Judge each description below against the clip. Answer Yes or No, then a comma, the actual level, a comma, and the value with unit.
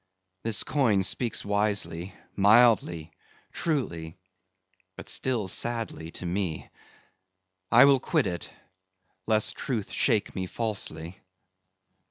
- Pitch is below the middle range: Yes, low, 105 Hz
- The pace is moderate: No, slow, 100 wpm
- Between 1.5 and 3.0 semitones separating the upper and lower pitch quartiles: No, average, 4.7 semitones